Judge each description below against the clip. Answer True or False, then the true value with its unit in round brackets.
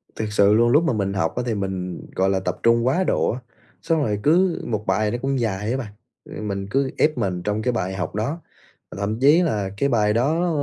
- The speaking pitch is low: True (110 Hz)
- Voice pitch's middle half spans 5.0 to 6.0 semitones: True (5.5 semitones)